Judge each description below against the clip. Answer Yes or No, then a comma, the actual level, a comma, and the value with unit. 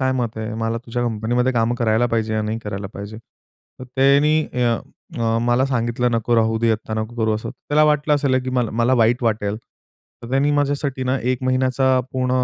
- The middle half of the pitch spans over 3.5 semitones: No, average, 2.7 semitones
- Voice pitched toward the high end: No, low, 120 Hz